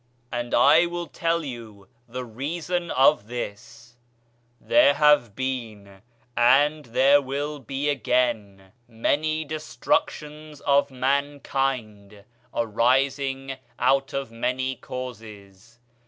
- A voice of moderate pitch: No, low, 130 Hz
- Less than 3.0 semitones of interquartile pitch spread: No, average, 3.8 semitones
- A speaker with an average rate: No, slow, 95 wpm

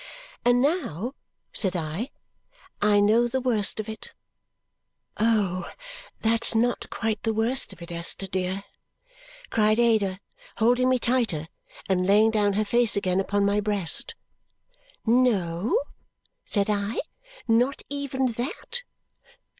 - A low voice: No, high, 215 Hz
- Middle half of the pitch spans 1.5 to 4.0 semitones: Yes, average, 3.5 semitones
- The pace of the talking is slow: Yes, slow, 120 wpm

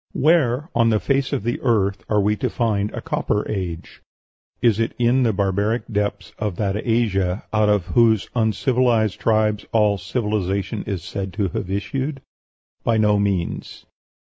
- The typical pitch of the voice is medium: No, low, 105 Hz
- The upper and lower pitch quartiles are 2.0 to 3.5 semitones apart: Yes, average, 2.8 semitones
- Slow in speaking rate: No, average, 160 wpm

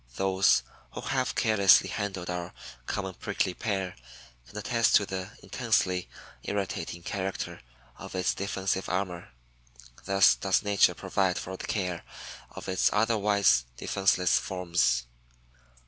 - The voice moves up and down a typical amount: No, narrow, 1.8 semitones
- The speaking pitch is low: Yes, very low, 95 Hz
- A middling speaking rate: No, slow, 120 wpm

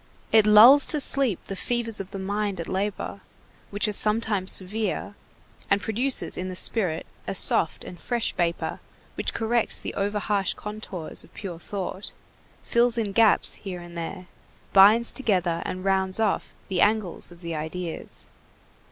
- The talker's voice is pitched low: No, high, 200 Hz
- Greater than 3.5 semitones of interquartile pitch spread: No, average, 3.2 semitones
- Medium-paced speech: Yes, average, 160 wpm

